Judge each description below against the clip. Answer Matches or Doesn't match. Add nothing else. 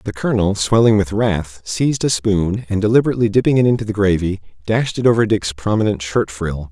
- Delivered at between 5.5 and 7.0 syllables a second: Matches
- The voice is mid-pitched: Doesn't match